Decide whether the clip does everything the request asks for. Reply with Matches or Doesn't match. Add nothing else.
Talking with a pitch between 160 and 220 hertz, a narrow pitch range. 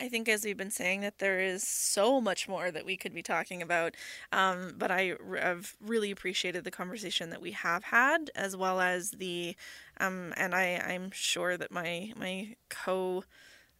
Matches